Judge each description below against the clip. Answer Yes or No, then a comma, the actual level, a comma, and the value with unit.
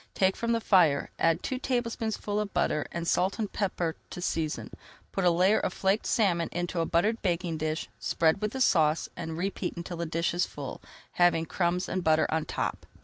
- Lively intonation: No, average, 3.4 semitones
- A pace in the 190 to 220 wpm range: Yes, average, 200 wpm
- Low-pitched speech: No, medium, 175 Hz